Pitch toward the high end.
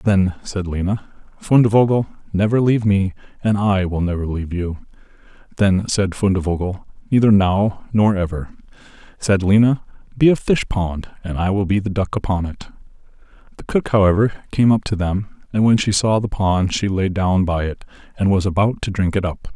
No: low, 100 Hz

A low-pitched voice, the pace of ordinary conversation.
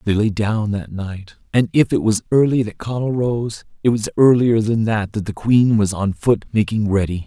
No: low, 110 Hz; fast, 215 wpm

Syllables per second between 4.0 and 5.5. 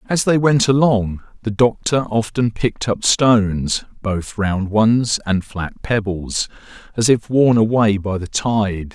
No: 3.8 syllables/s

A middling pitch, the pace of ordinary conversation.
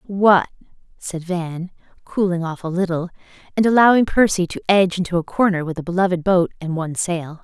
Yes: medium, 180 Hz; average, 180 wpm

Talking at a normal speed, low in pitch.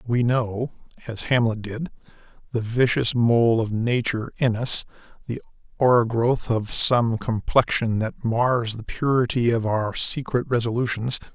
No: slow, 120 wpm; low, 120 Hz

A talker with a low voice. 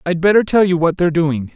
No: medium, 170 Hz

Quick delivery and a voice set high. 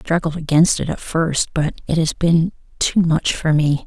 No: fast, 215 wpm; medium, 160 Hz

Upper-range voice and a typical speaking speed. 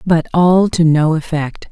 No: medium, 165 Hz; average, 175 wpm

